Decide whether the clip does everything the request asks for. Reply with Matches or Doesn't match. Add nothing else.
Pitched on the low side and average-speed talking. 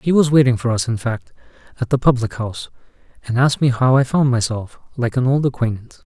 Doesn't match